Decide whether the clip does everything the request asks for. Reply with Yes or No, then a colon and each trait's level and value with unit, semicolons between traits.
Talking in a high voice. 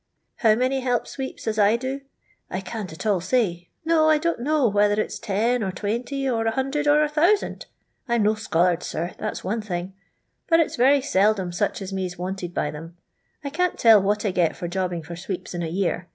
Yes: high, 210 Hz